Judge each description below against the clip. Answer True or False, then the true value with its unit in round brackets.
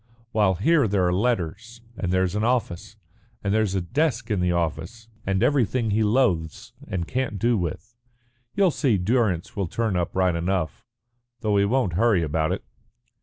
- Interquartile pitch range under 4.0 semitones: False (4.8 semitones)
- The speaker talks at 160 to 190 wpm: True (170 wpm)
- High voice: False (100 Hz)